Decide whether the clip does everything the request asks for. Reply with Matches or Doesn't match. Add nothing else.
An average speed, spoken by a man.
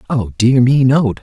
Doesn't match